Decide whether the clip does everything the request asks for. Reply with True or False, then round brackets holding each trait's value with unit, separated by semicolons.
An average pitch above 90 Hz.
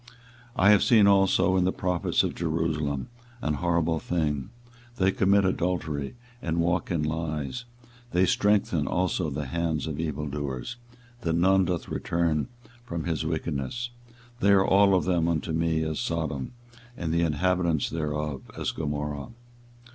False (85 Hz)